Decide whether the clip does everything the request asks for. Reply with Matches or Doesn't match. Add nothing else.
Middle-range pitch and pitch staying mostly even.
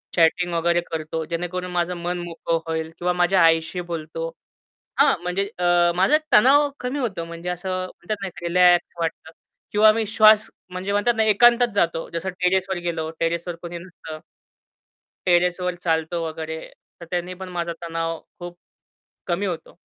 Matches